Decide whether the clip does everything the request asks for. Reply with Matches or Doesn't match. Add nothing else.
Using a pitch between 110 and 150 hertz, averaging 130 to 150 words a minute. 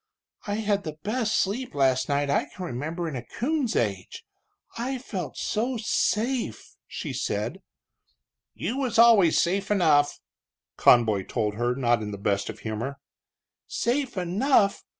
Doesn't match